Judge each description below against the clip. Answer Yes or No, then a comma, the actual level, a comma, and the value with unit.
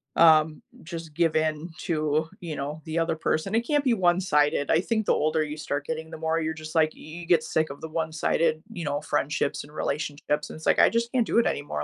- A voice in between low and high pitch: Yes, medium, 160 Hz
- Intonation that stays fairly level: Yes, narrow, 1.8 semitones